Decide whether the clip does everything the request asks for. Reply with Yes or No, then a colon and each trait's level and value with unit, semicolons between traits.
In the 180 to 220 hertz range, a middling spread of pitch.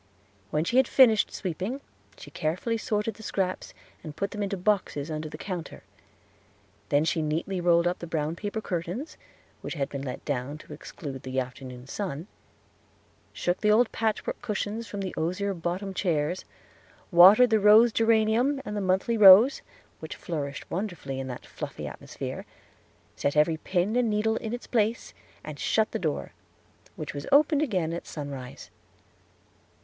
No: medium, 185 Hz; wide, 5.9 semitones